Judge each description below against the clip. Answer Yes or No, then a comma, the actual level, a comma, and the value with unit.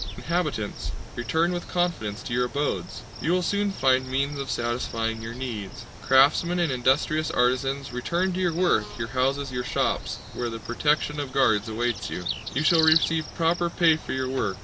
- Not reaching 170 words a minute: No, average, 175 wpm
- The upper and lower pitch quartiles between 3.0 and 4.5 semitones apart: No, average, 5.2 semitones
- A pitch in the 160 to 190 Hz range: No, low, 135 Hz